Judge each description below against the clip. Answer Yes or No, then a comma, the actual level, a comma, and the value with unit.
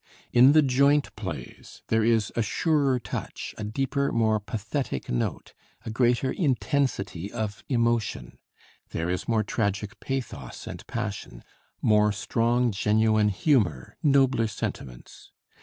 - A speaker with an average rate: No, slow, 125 wpm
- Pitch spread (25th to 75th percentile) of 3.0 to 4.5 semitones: Yes, average, 4.1 semitones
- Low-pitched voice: Yes, low, 110 Hz